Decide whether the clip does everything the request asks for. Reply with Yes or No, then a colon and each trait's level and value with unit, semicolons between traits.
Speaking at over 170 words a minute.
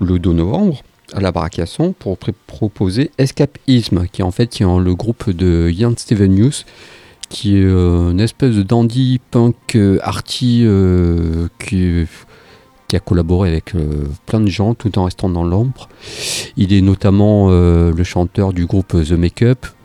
No: average, 165 wpm